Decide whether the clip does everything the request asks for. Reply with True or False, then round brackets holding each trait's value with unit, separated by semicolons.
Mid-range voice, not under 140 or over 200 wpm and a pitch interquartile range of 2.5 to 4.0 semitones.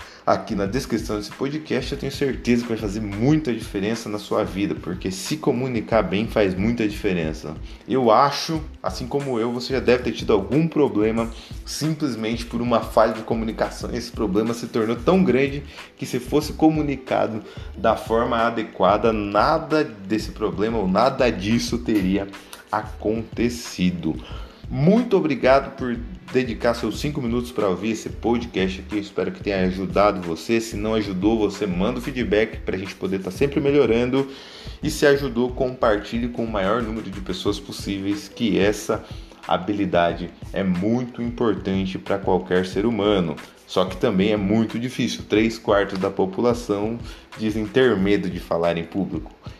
False (110 Hz; 160 wpm; 3.4 semitones)